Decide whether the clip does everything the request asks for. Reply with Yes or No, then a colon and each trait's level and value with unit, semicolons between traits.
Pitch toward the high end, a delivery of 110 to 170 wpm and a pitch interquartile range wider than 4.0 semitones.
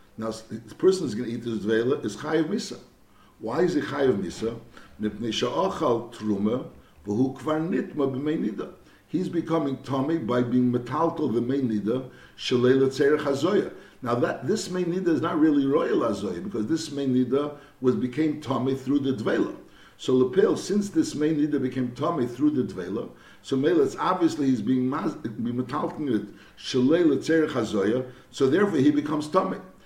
No: low, 135 Hz; average, 155 wpm; average, 4.8 semitones